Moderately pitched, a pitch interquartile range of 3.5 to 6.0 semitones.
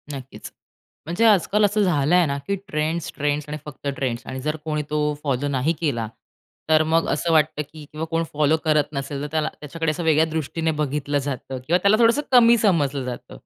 No: medium, 150 Hz; narrow, 2.5 semitones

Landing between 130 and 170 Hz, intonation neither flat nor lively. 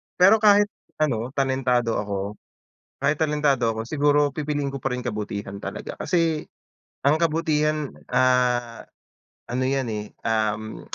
Yes: low, 135 Hz; average, 4.8 semitones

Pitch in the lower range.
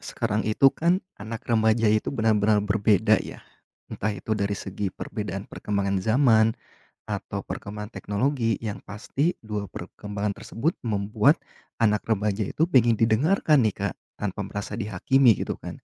Yes: low, 110 Hz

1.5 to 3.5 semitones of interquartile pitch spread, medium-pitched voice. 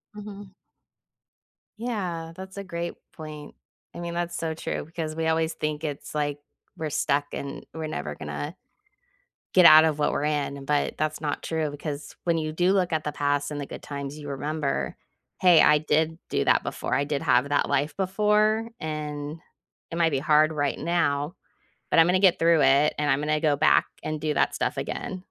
Yes: narrow, 2.6 semitones; medium, 155 Hz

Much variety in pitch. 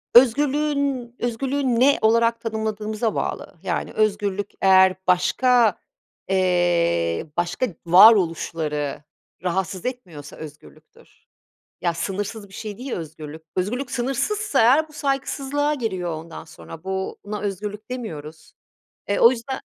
Yes: wide, 6.1 semitones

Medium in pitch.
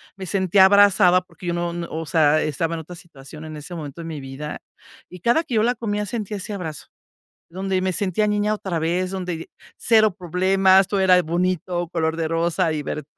Yes: medium, 180 Hz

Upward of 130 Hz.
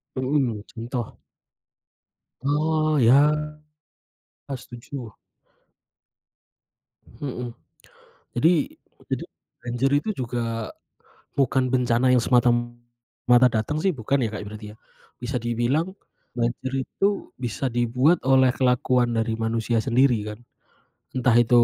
No: low, 125 Hz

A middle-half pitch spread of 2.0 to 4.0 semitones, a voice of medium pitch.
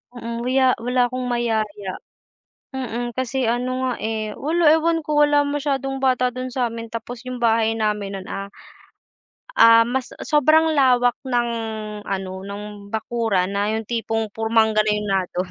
No: average, 3.2 semitones; high, 235 Hz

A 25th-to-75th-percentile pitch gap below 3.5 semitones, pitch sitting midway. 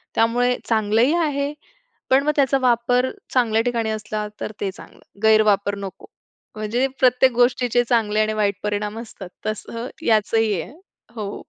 No: average, 2.7 semitones; high, 225 Hz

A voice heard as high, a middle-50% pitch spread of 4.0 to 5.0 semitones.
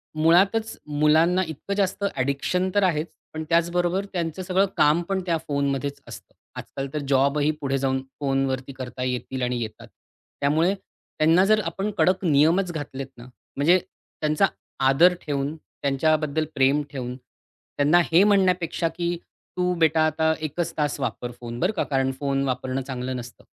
No: medium, 155 Hz; average, 4.4 semitones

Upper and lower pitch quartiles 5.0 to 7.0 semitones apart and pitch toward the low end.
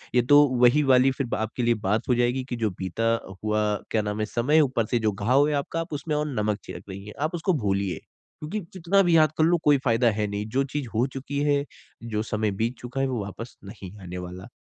Yes: average, 5.3 semitones; low, 120 Hz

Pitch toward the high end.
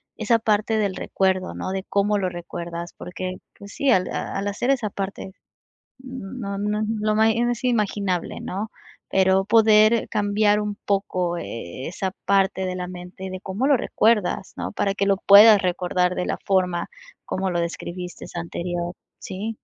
Yes: high, 195 Hz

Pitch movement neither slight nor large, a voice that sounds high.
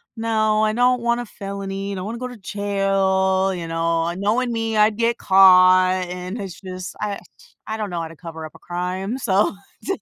Yes: average, 3.1 semitones; high, 195 Hz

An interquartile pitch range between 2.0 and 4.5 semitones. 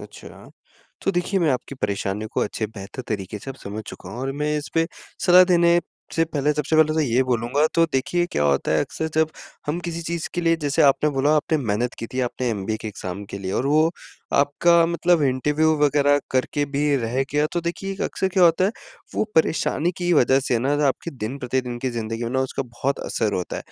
No: average, 5.3 semitones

